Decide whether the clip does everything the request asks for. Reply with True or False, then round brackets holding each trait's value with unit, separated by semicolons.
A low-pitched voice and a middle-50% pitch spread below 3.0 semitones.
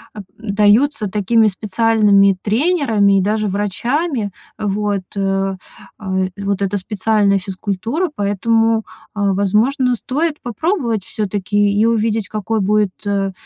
False (210 Hz; 2.4 semitones)